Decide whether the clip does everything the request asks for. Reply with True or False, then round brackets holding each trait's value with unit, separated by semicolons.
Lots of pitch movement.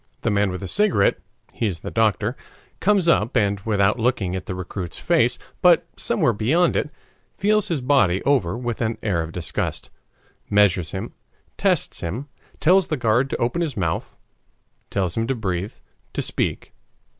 True (6.3 semitones)